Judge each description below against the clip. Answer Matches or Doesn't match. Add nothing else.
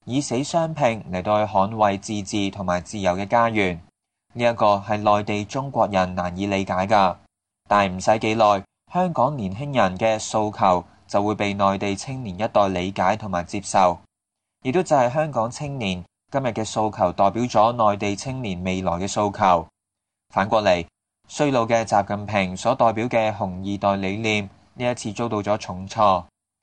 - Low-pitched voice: Matches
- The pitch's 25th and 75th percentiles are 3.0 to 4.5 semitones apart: Doesn't match